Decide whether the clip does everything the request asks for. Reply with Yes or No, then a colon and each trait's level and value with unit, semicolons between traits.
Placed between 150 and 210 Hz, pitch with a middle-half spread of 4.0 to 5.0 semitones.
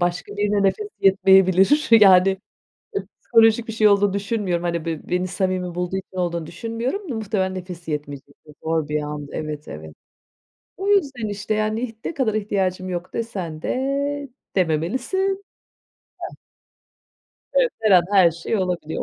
Yes: high, 190 Hz; average, 4.3 semitones